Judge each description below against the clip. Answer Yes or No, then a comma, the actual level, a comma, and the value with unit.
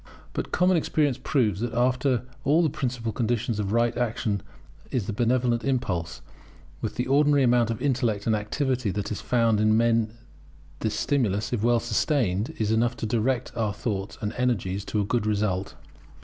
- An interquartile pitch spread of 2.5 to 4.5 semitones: Yes, average, 3.0 semitones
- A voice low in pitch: Yes, low, 115 Hz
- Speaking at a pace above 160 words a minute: Yes, average, 175 wpm